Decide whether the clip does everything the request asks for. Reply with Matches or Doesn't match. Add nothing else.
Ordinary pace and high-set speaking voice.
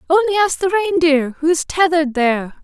Matches